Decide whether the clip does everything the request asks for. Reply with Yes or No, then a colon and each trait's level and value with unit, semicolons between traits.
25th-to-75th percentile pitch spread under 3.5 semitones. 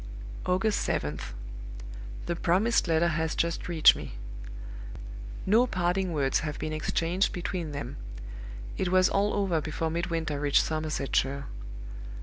Yes: average, 3.1 semitones